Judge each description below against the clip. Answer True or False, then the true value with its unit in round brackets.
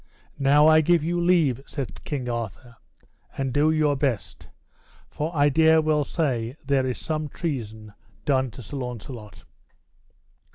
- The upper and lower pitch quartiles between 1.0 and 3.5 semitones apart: False (4.0 semitones)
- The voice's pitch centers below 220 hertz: True (140 Hz)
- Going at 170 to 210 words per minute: False (140 wpm)